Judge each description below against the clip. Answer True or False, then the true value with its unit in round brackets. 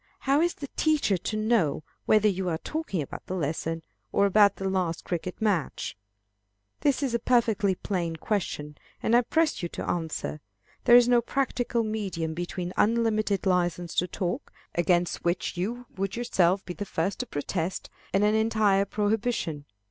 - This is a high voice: True (195 Hz)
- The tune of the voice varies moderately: True (4.6 semitones)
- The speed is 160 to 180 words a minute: True (170 wpm)